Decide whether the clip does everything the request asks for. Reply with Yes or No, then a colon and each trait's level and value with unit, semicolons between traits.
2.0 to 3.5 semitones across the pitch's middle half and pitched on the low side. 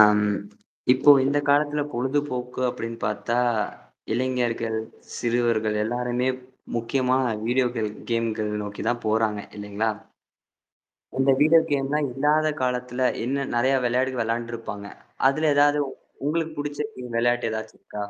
Yes: average, 3.2 semitones; low, 120 Hz